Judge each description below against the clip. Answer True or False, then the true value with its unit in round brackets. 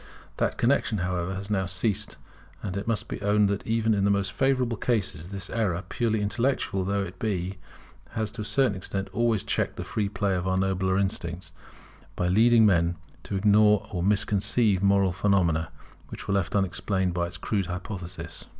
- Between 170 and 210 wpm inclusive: True (180 wpm)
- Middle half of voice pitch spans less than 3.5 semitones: True (2.6 semitones)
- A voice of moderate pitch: False (100 Hz)